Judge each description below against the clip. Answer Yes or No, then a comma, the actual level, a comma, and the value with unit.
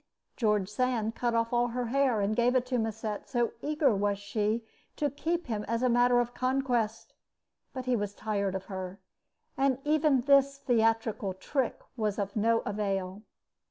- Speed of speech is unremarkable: Yes, average, 170 wpm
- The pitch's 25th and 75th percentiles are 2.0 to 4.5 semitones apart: Yes, average, 3.5 semitones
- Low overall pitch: No, high, 230 Hz